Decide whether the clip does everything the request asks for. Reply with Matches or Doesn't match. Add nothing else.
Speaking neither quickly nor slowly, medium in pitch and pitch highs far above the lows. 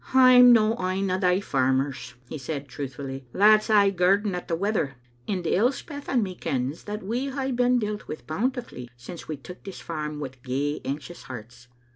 Matches